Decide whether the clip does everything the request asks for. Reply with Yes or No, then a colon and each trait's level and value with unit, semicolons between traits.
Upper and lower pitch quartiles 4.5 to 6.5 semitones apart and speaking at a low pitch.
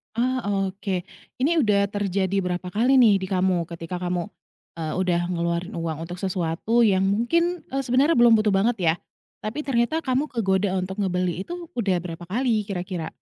No: average, 4.9 semitones; high, 195 Hz